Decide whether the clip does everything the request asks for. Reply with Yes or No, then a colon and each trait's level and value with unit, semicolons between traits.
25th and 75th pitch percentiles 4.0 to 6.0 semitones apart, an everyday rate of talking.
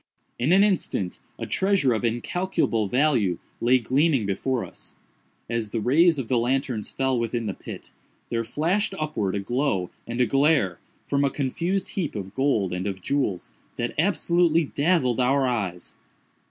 Yes: wide, 5.5 semitones; average, 160 wpm